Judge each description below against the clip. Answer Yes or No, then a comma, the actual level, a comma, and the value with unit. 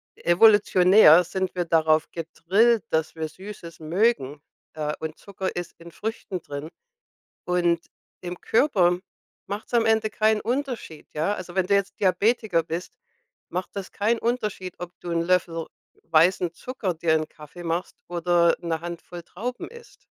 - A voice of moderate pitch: Yes, medium, 180 Hz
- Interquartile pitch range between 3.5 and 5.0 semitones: Yes, average, 3.8 semitones